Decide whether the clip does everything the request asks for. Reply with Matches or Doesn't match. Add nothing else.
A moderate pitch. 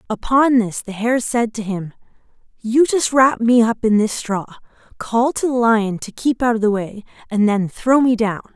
Doesn't match